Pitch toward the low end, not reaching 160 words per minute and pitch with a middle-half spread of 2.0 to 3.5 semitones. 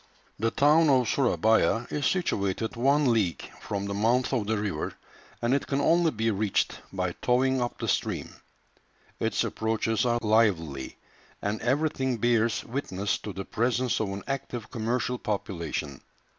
No: low, 115 Hz; average, 150 wpm; average, 4.0 semitones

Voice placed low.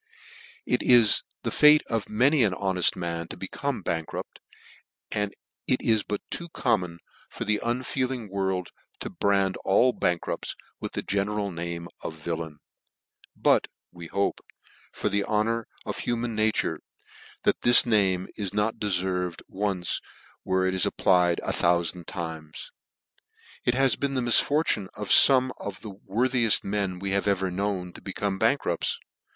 Yes: low, 100 Hz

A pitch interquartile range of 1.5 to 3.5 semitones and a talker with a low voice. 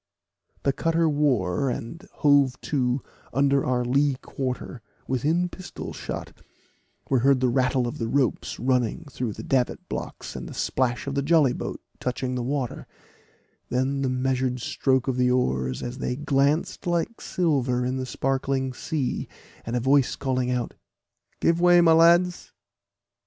Yes: narrow, 2.5 semitones; low, 130 Hz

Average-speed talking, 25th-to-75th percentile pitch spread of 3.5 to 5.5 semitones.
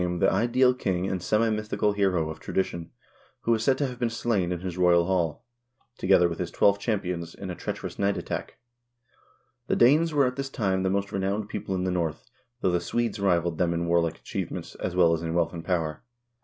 No: fast, 225 wpm; average, 3.8 semitones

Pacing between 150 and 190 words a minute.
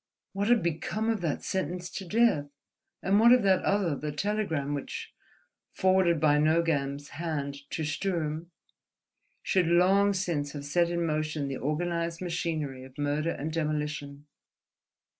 No: average, 140 wpm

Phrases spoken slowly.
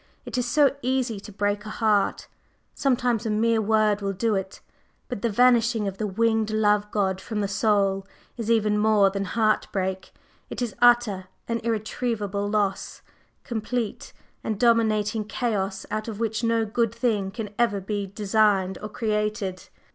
No: average, 160 wpm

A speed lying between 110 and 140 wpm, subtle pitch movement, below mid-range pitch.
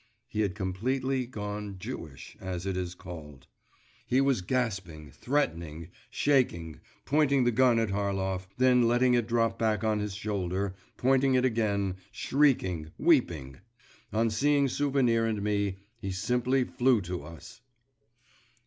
No: slow, 135 wpm; average, 5.3 semitones; low, 110 Hz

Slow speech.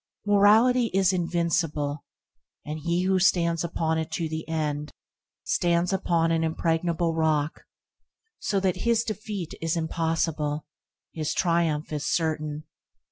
Yes: slow, 120 wpm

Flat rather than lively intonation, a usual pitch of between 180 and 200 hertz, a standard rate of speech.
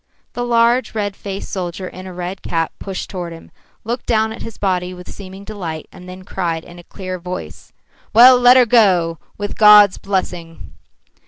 No: average, 3.3 semitones; high, 190 Hz; average, 180 wpm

